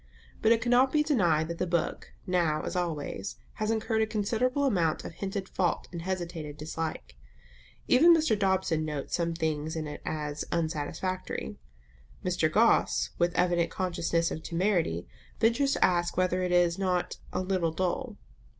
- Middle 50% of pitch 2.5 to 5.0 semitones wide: Yes, average, 4.1 semitones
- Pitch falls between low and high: Yes, medium, 175 Hz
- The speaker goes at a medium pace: Yes, average, 160 wpm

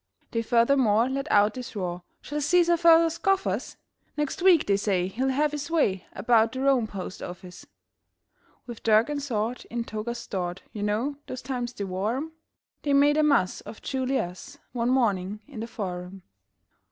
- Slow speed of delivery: No, average, 175 wpm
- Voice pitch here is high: Yes, high, 235 Hz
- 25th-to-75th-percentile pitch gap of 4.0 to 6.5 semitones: Yes, wide, 5.5 semitones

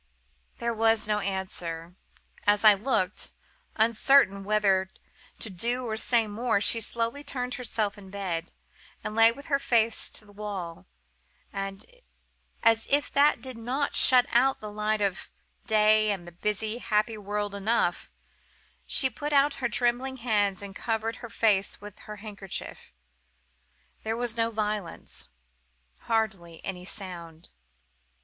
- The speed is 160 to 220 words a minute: No, average, 140 wpm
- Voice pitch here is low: No, high, 215 Hz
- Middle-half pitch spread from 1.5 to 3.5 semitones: Yes, average, 2.9 semitones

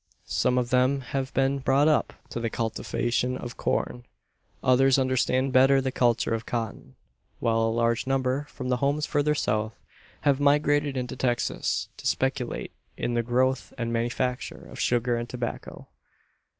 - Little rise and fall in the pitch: Yes, narrow, 2.2 semitones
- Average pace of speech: Yes, average, 150 wpm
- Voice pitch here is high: No, low, 125 Hz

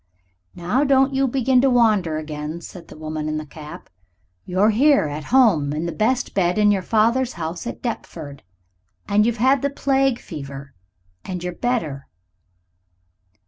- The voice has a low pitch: No, high, 195 Hz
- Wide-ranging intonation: Yes, wide, 8.2 semitones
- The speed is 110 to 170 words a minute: Yes, average, 160 wpm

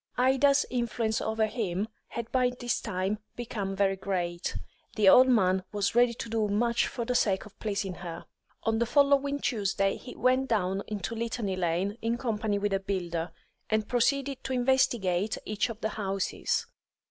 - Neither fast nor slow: Yes, average, 170 wpm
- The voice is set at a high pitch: Yes, high, 220 Hz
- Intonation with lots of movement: No, average, 3.8 semitones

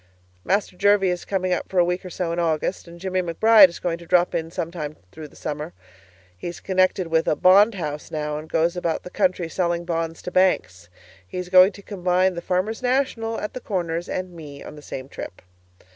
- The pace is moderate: No, fast, 210 wpm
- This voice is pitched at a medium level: Yes, medium, 180 Hz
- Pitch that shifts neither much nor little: No, narrow, 2.3 semitones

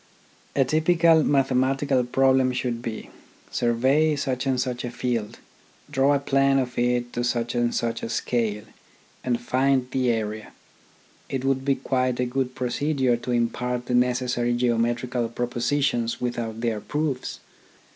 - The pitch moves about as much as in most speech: No, narrow, 2.0 semitones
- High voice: No, low, 125 Hz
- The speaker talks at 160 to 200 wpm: No, average, 145 wpm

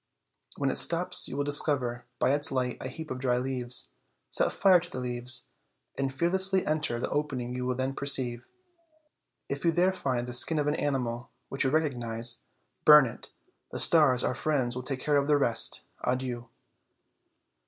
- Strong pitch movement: No, average, 3.1 semitones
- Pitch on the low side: Yes, low, 130 Hz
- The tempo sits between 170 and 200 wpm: Yes, average, 180 wpm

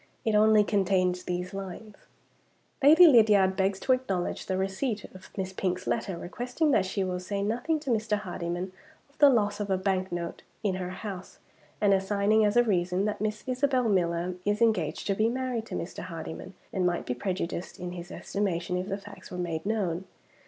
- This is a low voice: No, high, 195 Hz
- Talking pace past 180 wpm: Yes, average, 190 wpm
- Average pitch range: Yes, average, 3.1 semitones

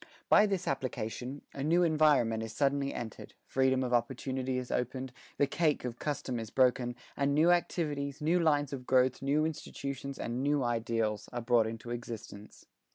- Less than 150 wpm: No, average, 165 wpm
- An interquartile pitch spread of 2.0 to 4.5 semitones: Yes, average, 3.3 semitones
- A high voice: No, low, 130 Hz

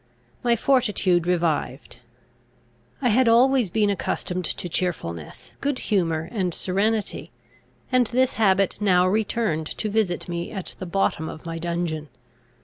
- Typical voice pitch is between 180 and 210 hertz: Yes, high, 190 Hz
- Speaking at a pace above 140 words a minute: No, slow, 135 wpm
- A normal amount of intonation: Yes, average, 4.6 semitones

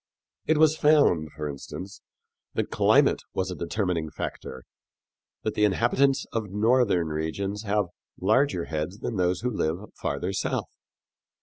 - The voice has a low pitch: Yes, very low, 95 Hz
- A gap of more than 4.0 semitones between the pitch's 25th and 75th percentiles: Yes, wide, 5.5 semitones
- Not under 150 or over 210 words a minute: No, slow, 135 wpm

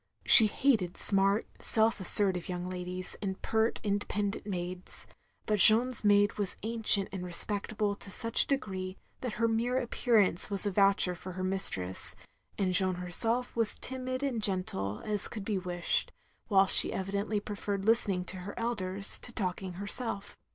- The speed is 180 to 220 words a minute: No, average, 160 wpm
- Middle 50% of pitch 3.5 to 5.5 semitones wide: No, average, 3.1 semitones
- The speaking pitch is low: No, high, 200 Hz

